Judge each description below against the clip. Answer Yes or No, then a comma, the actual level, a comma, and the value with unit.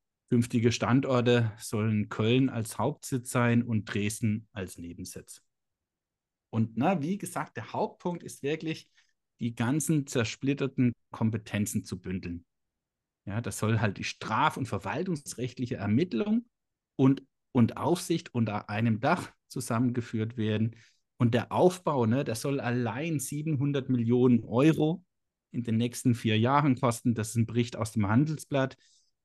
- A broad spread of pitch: No, average, 3.9 semitones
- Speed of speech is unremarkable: Yes, average, 135 wpm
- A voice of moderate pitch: No, low, 120 Hz